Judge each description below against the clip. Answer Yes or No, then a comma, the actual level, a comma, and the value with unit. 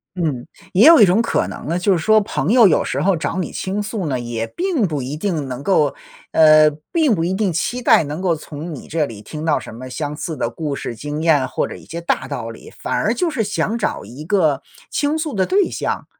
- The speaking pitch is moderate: Yes, medium, 165 Hz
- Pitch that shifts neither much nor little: No, wide, 6.2 semitones